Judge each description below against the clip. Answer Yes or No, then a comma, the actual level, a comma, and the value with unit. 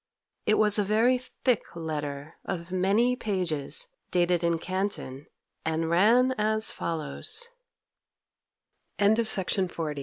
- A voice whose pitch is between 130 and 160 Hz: No, medium, 185 Hz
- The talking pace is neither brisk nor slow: No, slow, 110 wpm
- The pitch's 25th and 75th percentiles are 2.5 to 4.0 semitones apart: No, average, 4.9 semitones